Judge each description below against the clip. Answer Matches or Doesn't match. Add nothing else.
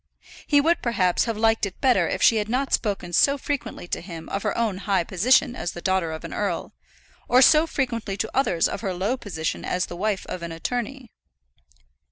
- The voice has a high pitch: Matches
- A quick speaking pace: Matches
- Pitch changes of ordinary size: Doesn't match